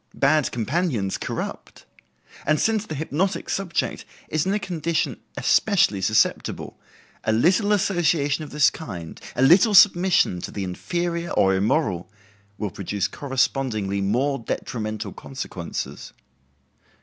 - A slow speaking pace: Yes, slow, 120 wpm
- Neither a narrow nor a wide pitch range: No, wide, 8.5 semitones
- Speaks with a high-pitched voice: No, medium, 140 Hz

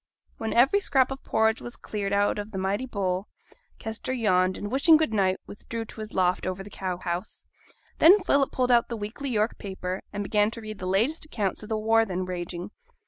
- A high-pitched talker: Yes, high, 215 Hz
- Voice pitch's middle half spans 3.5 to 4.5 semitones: Yes, average, 3.9 semitones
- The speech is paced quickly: Yes, fast, 210 wpm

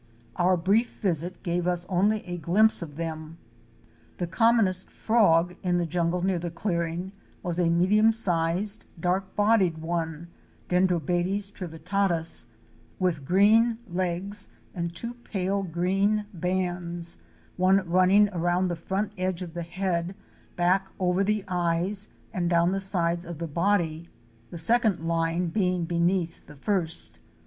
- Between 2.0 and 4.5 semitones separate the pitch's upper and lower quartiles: Yes, narrow, 2.4 semitones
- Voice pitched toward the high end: No, medium, 180 Hz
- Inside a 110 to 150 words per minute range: Yes, average, 140 wpm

